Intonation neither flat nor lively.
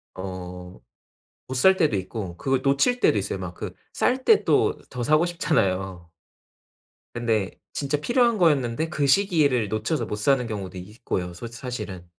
No: wide, 8.1 semitones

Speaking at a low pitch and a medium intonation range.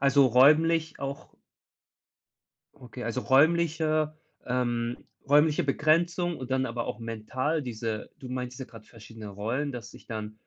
Yes: low, 130 Hz; average, 4.6 semitones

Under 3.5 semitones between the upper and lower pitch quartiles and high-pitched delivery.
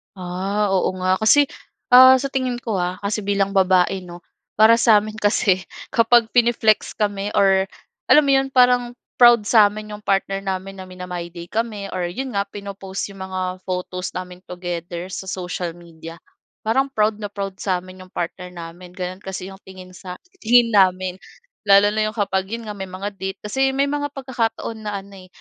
Yes: average, 3.1 semitones; high, 195 Hz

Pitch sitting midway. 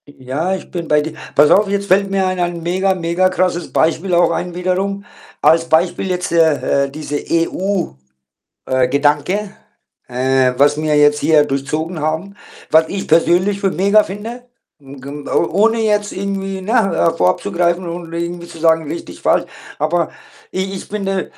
Yes: medium, 170 Hz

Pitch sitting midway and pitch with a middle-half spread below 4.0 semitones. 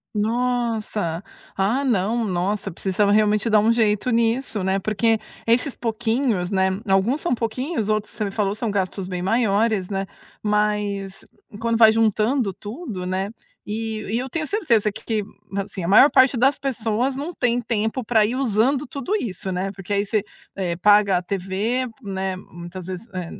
No: high, 215 Hz; average, 3.3 semitones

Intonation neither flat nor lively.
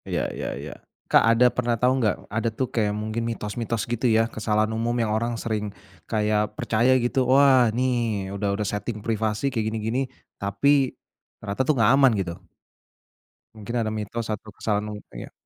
No: narrow, 2.2 semitones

